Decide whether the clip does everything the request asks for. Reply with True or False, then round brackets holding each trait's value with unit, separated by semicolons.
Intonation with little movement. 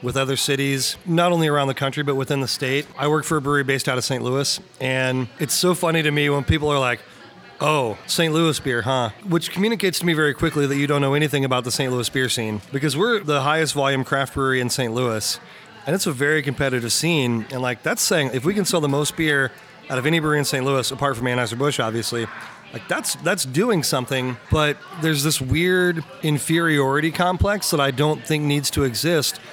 False (3.3 semitones)